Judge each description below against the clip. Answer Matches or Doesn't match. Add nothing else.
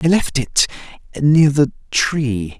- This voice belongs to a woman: Doesn't match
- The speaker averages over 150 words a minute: Doesn't match